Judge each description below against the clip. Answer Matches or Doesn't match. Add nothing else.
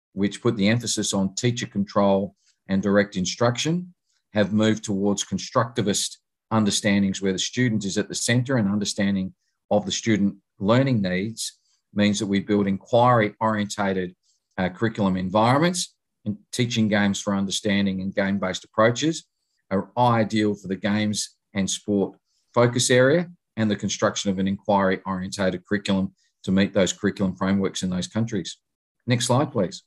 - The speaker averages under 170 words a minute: Matches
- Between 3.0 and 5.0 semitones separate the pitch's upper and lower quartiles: Doesn't match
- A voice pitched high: Doesn't match